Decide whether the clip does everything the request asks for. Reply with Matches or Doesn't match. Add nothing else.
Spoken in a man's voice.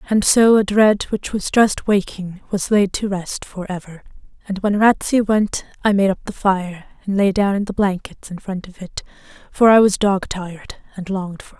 Doesn't match